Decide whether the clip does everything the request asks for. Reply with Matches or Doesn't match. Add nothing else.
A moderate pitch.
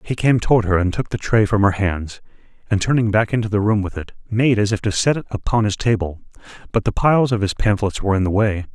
Doesn't match